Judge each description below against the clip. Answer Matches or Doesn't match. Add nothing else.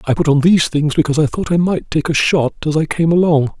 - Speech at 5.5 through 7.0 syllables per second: Matches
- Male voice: Matches